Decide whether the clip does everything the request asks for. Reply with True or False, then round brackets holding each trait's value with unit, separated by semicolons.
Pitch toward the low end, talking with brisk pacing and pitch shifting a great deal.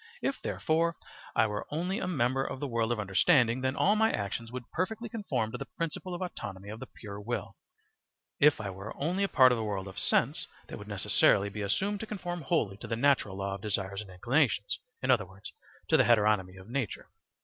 True (120 Hz; 215 wpm; 8.1 semitones)